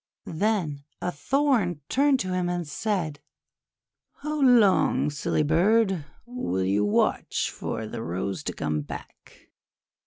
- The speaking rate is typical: No, slow, 130 wpm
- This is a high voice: No, medium, 175 Hz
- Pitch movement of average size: No, wide, 7.9 semitones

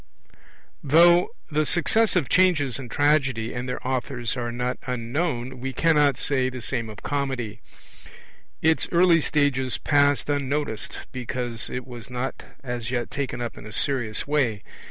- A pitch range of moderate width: Yes, average, 3.1 semitones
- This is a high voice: No, low, 130 Hz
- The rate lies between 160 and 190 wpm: No, average, 145 wpm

